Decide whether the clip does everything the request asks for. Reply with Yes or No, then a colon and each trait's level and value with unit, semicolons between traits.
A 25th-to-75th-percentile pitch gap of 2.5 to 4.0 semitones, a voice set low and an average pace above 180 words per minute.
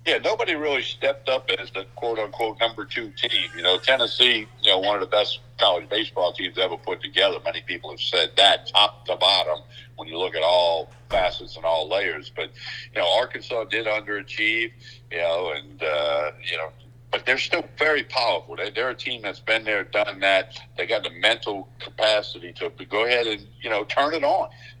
Yes: average, 2.8 semitones; low, 115 Hz; average, 200 wpm